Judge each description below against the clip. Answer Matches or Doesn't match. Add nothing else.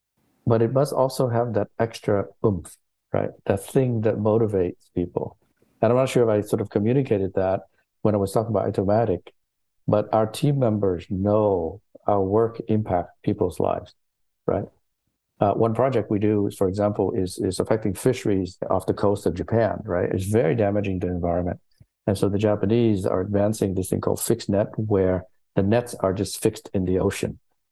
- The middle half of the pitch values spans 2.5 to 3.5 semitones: Matches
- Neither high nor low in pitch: Doesn't match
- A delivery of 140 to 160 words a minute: Doesn't match